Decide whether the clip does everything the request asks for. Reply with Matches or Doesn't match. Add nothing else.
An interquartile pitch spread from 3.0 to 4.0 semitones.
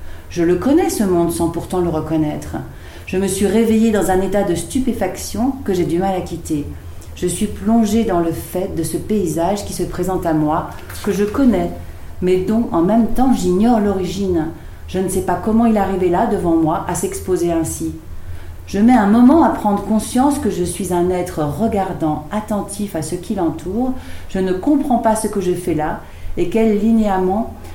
Doesn't match